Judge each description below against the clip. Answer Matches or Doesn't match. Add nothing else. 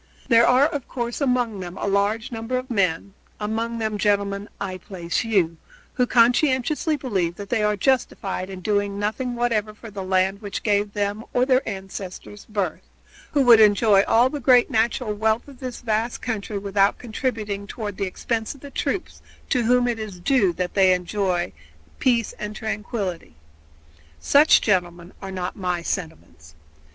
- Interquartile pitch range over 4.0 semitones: Doesn't match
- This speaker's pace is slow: Doesn't match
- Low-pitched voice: Doesn't match